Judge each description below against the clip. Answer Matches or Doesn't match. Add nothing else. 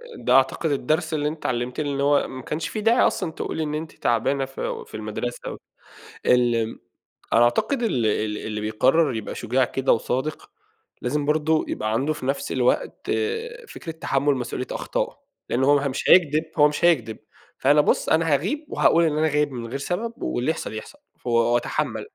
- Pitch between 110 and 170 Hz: Matches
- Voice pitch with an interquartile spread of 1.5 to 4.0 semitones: Doesn't match